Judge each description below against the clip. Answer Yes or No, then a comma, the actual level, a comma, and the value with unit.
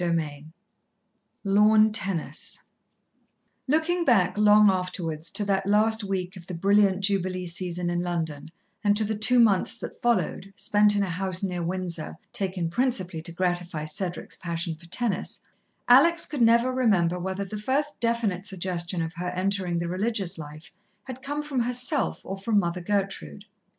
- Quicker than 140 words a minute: Yes, average, 155 wpm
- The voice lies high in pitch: Yes, high, 195 Hz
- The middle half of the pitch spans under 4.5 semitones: Yes, average, 3.7 semitones